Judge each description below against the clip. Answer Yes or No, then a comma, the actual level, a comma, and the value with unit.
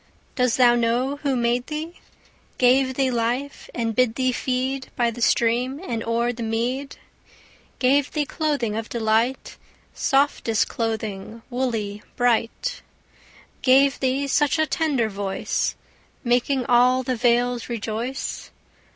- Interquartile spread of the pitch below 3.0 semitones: Yes, narrow, 2.6 semitones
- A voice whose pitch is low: No, high, 245 Hz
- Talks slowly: Yes, slow, 125 wpm